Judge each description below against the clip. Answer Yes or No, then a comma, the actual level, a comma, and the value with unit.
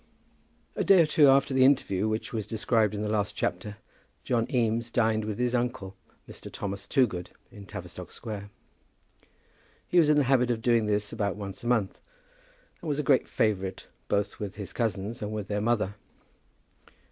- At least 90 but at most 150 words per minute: No, average, 180 wpm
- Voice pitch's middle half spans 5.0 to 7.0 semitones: No, average, 3.3 semitones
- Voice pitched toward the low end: Yes, low, 110 Hz